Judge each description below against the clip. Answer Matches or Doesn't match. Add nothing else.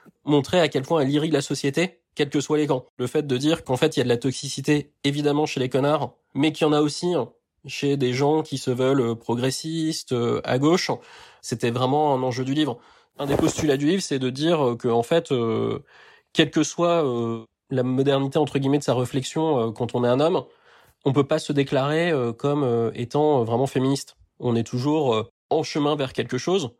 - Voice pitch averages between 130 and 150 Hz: Matches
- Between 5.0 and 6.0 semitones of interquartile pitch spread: Doesn't match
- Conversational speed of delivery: Doesn't match